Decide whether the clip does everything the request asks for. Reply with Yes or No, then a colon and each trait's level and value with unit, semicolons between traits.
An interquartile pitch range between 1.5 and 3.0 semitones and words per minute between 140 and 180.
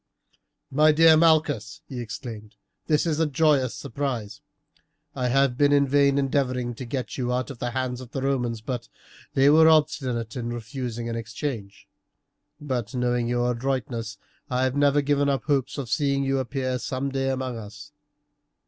Yes: average, 2.7 semitones; average, 165 wpm